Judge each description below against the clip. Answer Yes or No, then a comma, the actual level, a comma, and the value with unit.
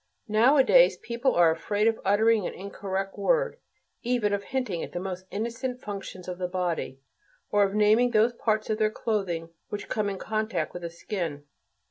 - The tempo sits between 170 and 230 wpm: Yes, average, 175 wpm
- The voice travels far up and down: No, average, 3.8 semitones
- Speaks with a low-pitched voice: No, high, 210 Hz